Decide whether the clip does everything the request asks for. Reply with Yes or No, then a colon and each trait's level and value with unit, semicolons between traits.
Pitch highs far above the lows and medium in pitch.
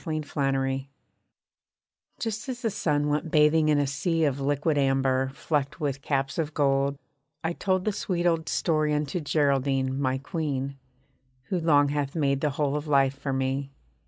No: narrow, 2.5 semitones; medium, 145 Hz